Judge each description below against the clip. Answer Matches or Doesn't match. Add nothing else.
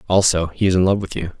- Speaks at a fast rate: Matches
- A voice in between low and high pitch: Doesn't match